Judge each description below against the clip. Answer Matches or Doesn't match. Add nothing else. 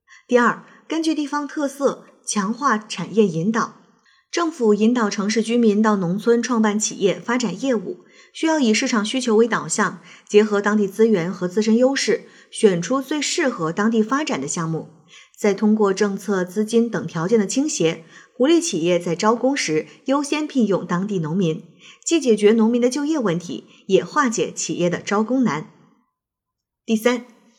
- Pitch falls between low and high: Doesn't match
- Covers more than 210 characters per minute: Matches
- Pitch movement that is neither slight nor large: Matches